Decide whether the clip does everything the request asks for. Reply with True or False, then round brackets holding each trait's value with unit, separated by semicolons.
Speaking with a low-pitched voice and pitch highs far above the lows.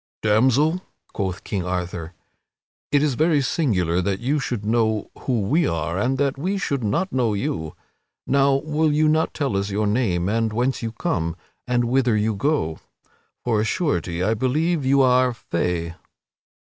True (120 Hz; 6.1 semitones)